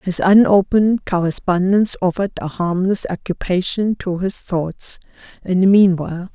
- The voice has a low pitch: No, medium, 185 Hz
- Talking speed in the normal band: No, slow, 125 wpm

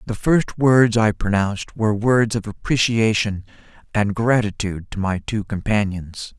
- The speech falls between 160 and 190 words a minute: No, average, 140 wpm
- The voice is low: Yes, low, 110 Hz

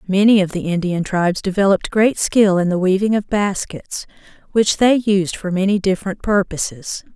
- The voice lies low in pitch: No, high, 195 Hz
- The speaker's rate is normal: Yes, average, 170 wpm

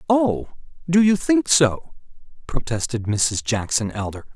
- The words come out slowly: Yes, slow, 125 wpm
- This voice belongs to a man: Yes, male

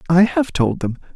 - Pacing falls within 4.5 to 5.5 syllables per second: Yes, 4.9 syllables/s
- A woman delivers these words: No, male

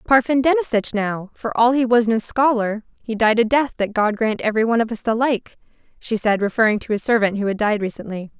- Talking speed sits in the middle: No, fast, 230 wpm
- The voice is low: No, high, 225 Hz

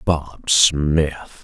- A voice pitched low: Yes, very low, 75 Hz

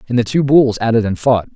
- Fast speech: Yes, fast, 310 wpm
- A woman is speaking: No, male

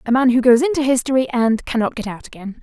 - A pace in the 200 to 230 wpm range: No, fast, 250 wpm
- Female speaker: Yes, female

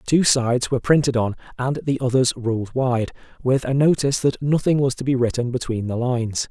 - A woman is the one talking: No, male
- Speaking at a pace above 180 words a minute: Yes, fast, 205 wpm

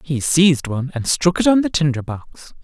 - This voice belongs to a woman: No, male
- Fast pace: Yes, fast, 230 wpm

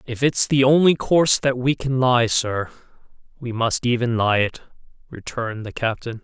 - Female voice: No, male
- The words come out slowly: No, average, 175 wpm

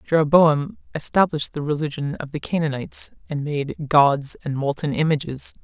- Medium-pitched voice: Yes, medium, 150 Hz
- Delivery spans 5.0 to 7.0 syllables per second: Yes, 5.2 syllables/s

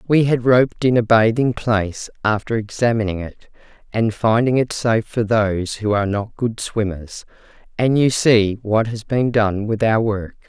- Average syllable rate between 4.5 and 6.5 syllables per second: Yes, 4.7 syllables/s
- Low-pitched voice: Yes, low, 110 Hz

